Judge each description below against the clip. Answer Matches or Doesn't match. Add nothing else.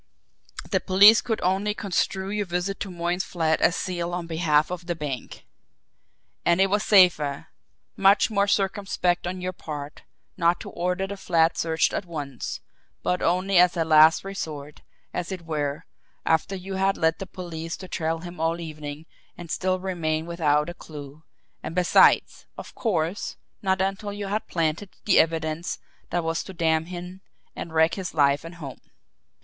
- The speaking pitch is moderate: Matches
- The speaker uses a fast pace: Doesn't match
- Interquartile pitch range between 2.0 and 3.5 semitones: Matches